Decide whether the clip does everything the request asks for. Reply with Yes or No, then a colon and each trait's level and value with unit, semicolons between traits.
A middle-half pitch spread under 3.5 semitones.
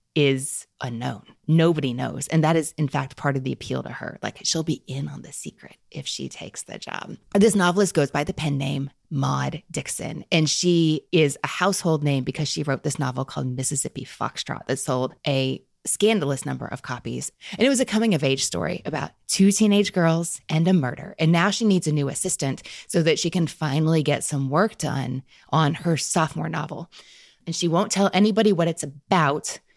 No: average, 4.3 semitones